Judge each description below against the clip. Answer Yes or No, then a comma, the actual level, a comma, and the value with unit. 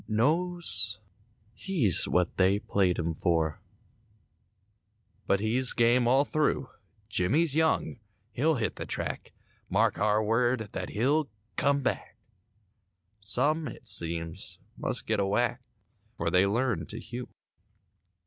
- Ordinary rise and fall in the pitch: No, wide, 5.8 semitones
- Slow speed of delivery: Yes, slow, 120 wpm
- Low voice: Yes, low, 115 Hz